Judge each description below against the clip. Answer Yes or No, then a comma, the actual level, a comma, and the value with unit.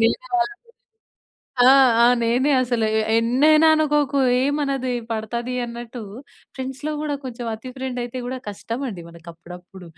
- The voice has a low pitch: No, very high, 250 Hz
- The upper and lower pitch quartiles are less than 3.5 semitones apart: No, average, 3.8 semitones